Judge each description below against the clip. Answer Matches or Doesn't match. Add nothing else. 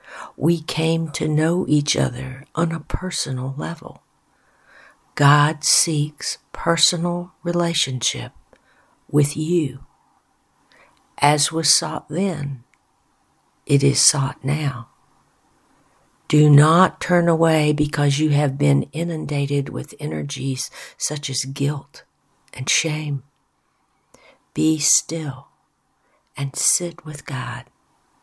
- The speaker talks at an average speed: Doesn't match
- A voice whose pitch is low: Doesn't match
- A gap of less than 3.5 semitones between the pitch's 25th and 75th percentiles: Matches